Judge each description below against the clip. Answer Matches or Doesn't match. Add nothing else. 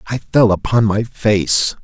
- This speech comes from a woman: Doesn't match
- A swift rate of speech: Doesn't match